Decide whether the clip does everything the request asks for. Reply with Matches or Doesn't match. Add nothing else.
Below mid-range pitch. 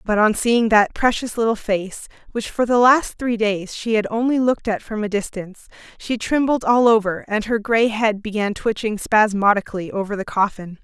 Doesn't match